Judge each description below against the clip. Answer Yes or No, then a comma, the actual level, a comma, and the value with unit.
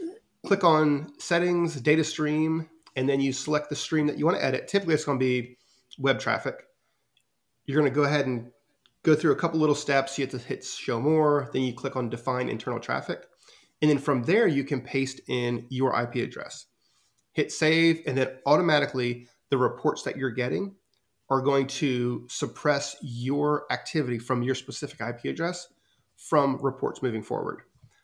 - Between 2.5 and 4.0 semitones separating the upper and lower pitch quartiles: Yes, average, 3.1 semitones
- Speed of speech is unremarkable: Yes, average, 180 wpm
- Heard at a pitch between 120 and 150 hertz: Yes, medium, 140 Hz